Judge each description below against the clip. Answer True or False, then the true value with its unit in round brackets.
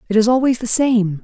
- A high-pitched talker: True (230 Hz)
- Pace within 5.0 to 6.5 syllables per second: True (5.5 syllables/s)